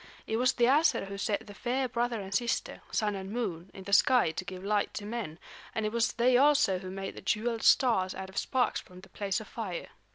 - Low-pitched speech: No, high, 210 Hz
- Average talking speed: No, fast, 235 wpm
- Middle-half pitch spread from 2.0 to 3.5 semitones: No, average, 3.9 semitones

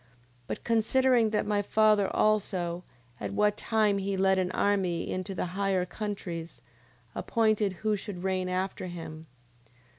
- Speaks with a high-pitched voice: Yes, high, 195 Hz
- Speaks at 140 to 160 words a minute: Yes, average, 150 wpm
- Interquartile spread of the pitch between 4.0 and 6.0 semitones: No, average, 2.7 semitones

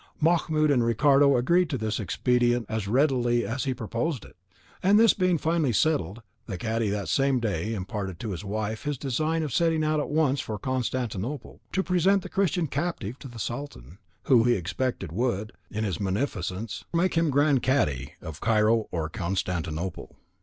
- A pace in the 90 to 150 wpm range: No, average, 175 wpm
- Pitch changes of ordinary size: No, wide, 6.3 semitones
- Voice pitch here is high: No, low, 120 Hz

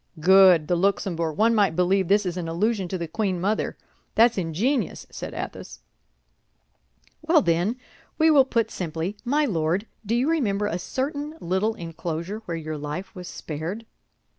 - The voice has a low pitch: No, high, 190 Hz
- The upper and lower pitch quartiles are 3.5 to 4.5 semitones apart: No, average, 5.0 semitones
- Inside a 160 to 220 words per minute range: Yes, average, 165 wpm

